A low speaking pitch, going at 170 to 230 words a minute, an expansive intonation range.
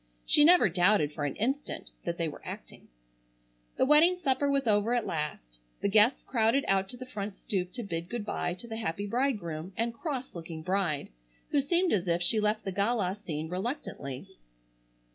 No: high, 205 Hz; average, 185 wpm; wide, 6.1 semitones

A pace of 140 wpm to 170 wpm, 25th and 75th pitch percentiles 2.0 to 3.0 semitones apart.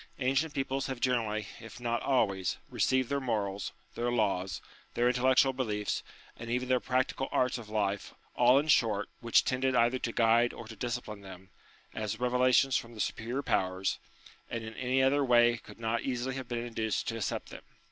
No: average, 185 wpm; average, 2.7 semitones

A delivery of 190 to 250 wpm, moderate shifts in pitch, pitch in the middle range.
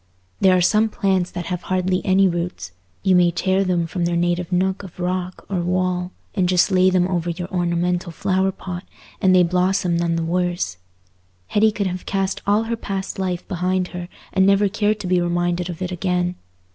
No: average, 195 wpm; narrow, 1.3 semitones; medium, 180 Hz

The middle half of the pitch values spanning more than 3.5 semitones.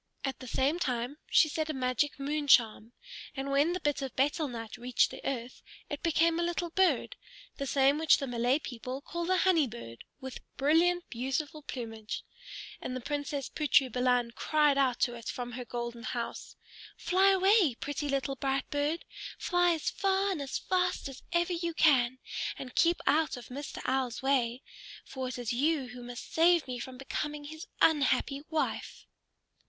Yes: average, 4.2 semitones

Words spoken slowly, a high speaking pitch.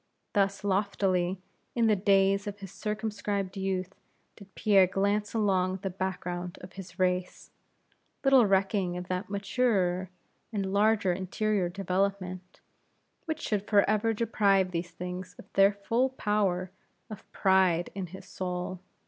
Yes: slow, 130 wpm; high, 195 Hz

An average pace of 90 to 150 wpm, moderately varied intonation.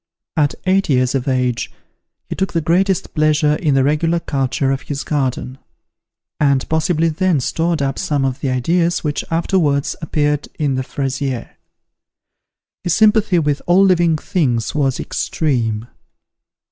Yes: average, 145 wpm; average, 4.0 semitones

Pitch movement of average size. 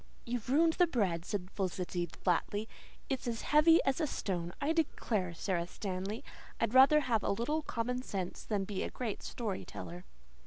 No: wide, 6.2 semitones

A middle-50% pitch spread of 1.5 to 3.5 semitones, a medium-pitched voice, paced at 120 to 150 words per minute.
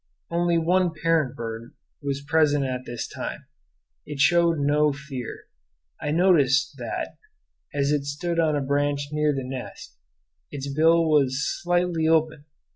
Yes: average, 2.9 semitones; medium, 145 Hz; average, 140 wpm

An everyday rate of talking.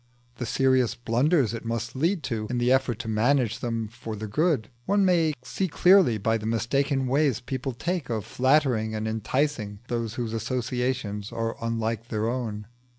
Yes: average, 170 wpm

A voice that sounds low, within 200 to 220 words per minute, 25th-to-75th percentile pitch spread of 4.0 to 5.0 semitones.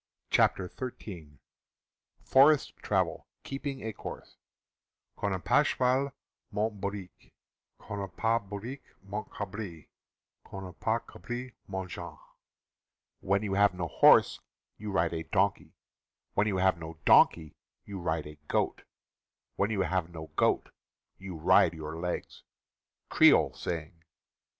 No: very low, 95 Hz; slow, 135 wpm; average, 4.3 semitones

